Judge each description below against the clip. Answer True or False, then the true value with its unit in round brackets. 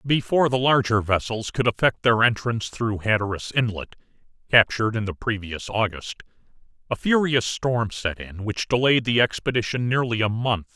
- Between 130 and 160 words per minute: True (155 wpm)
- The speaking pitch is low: True (115 Hz)